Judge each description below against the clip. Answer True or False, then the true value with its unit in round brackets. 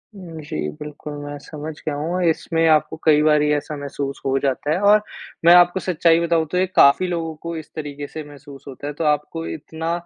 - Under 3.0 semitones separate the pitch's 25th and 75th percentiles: True (2.4 semitones)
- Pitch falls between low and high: True (155 Hz)